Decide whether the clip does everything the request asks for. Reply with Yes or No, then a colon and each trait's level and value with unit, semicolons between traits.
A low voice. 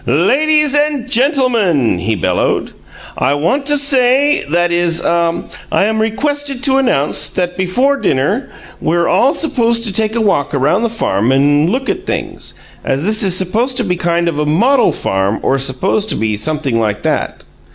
No: high, 195 Hz